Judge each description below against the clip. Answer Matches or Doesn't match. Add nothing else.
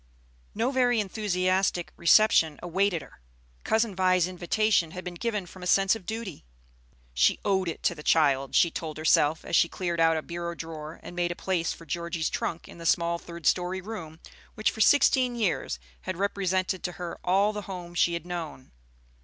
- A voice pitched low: Doesn't match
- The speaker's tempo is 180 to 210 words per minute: Matches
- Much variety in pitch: Doesn't match